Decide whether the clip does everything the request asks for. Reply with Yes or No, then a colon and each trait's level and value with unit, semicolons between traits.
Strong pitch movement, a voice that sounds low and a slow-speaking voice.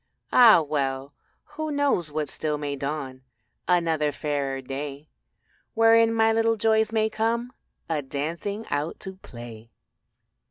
No: wide, 7.8 semitones; medium, 160 Hz; slow, 125 wpm